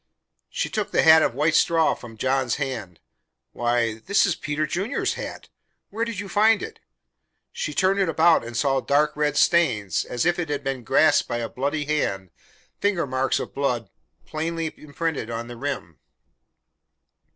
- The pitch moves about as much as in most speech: No, wide, 5.7 semitones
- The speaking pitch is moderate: Yes, medium, 145 Hz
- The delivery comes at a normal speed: Yes, average, 170 wpm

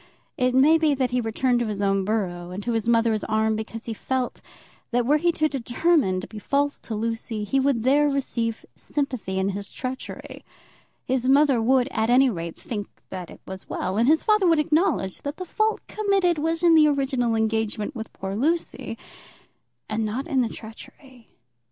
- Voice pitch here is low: No, high, 245 Hz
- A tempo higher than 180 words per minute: Yes, average, 190 wpm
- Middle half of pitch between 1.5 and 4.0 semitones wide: No, average, 4.8 semitones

